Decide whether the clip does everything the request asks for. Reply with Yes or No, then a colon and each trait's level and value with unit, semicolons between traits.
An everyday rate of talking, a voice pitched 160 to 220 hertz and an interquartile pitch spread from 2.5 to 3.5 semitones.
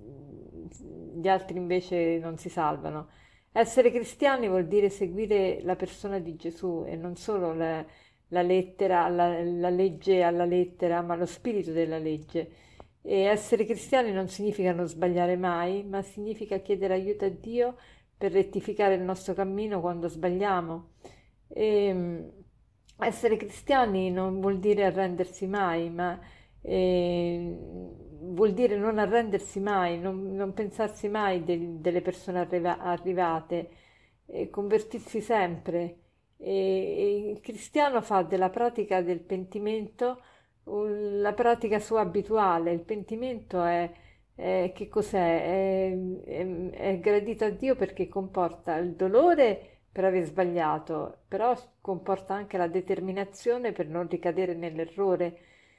Yes: average, 130 wpm; high, 190 Hz; average, 2.8 semitones